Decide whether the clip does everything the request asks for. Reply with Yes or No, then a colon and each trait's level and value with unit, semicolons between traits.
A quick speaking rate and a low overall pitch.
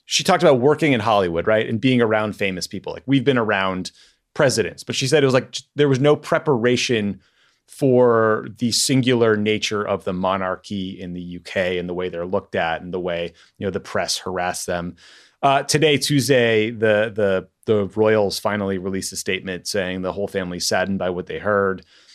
No: average, 195 wpm; low, 110 Hz